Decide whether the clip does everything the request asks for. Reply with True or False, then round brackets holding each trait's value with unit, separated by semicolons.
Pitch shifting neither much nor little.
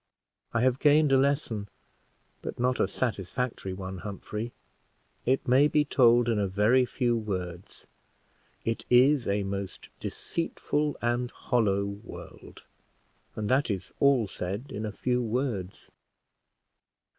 True (4.4 semitones)